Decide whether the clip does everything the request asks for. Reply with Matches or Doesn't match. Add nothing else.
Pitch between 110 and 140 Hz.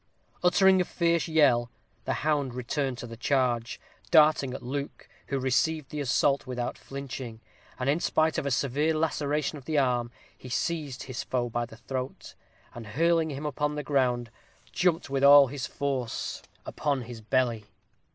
Matches